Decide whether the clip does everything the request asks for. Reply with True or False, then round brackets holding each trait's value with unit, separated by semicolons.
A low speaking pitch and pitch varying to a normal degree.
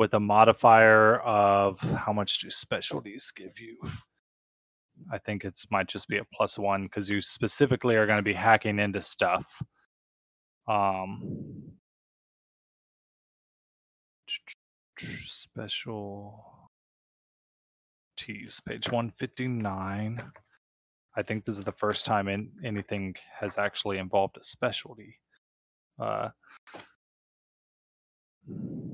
False (105 Hz; 2.1 semitones)